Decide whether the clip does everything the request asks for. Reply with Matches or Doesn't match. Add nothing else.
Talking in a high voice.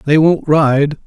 Doesn't match